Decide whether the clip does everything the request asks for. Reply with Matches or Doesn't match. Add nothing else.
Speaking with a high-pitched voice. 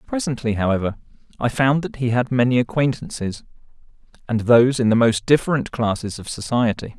Doesn't match